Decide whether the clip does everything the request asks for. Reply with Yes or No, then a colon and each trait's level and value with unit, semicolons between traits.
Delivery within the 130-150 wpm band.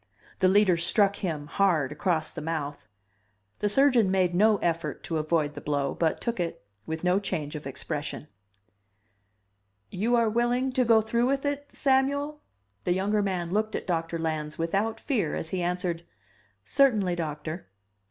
No: average, 160 wpm